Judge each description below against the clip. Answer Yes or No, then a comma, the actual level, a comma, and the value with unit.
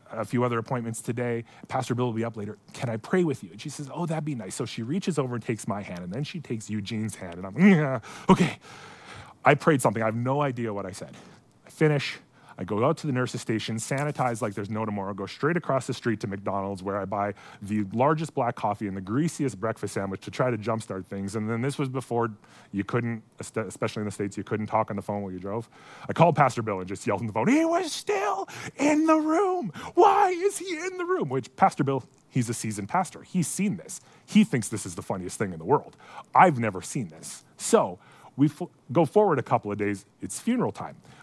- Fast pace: Yes, fast, 245 wpm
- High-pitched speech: No, low, 120 Hz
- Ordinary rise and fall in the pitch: No, wide, 6.3 semitones